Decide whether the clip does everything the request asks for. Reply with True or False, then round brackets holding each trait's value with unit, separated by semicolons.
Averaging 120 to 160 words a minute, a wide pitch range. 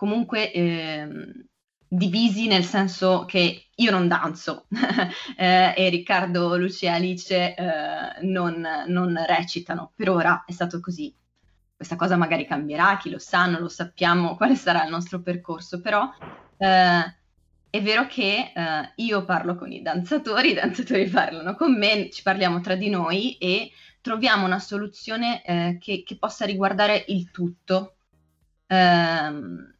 False (145 wpm; 3.0 semitones)